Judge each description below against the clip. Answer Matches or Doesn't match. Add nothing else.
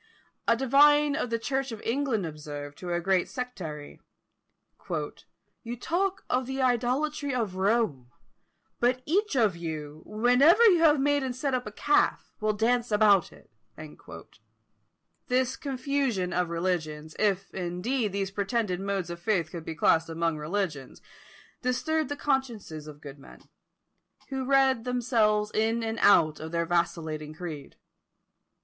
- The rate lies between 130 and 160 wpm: Matches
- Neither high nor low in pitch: Doesn't match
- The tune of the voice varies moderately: Doesn't match